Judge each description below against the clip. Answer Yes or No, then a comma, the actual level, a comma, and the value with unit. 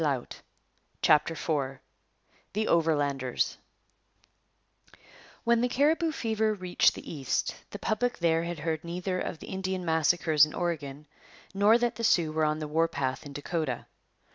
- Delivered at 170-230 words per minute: No, average, 140 wpm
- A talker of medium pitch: Yes, medium, 165 Hz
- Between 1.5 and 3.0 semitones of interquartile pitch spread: No, average, 5.0 semitones